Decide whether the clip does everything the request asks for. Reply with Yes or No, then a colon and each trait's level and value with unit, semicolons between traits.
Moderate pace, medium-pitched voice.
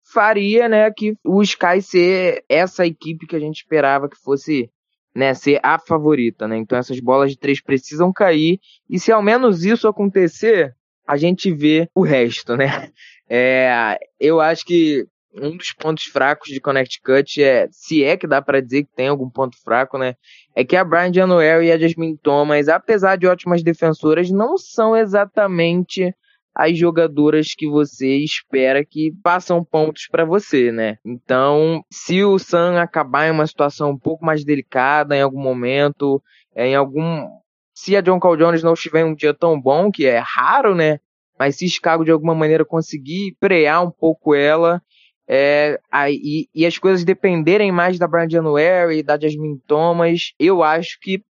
Yes: average, 175 wpm; medium, 160 Hz